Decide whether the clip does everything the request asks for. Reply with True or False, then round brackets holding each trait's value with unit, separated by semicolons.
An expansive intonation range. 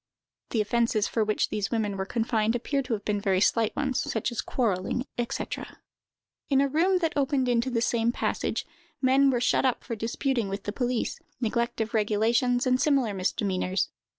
False (3.4 semitones)